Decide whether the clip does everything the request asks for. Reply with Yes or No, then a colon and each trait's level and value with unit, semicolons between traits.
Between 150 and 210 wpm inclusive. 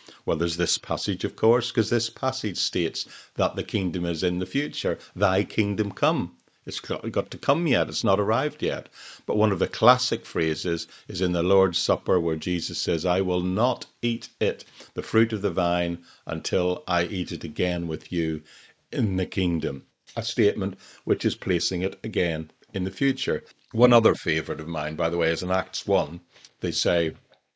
Yes: average, 190 wpm